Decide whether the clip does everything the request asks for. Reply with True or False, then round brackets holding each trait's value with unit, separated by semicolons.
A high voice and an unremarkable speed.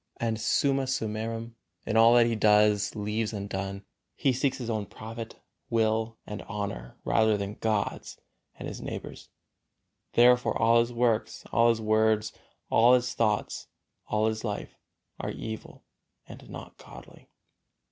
False (110 Hz; 145 wpm)